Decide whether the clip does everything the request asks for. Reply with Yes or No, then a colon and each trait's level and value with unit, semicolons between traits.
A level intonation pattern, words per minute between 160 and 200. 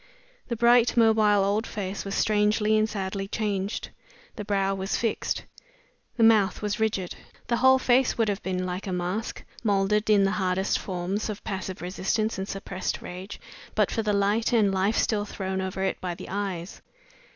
Yes: narrow, 2.2 semitones; average, 175 wpm